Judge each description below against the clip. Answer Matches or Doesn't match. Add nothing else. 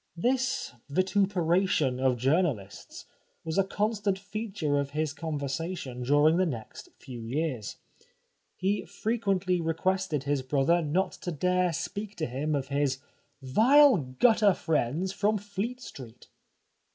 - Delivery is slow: Matches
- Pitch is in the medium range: Matches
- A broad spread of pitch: Matches